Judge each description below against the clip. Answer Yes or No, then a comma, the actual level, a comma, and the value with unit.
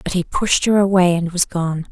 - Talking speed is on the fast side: Yes, fast, 250 wpm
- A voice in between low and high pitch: Yes, medium, 180 Hz